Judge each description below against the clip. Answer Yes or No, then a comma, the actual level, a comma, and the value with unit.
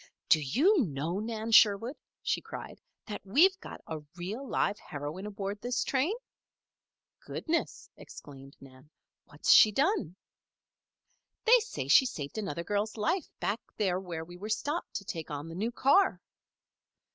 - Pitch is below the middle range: No, high, 205 Hz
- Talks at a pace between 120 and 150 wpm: Yes, average, 145 wpm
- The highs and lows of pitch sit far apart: Yes, wide, 7.9 semitones